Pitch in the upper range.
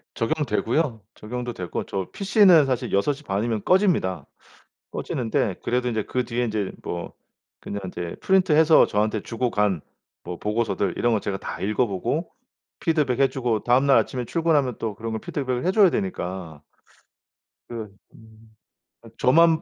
No: low, 120 Hz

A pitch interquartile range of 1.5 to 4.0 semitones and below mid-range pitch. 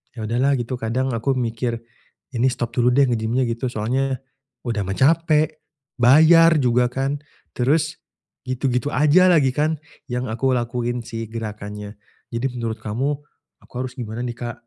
Yes: average, 2.7 semitones; low, 125 Hz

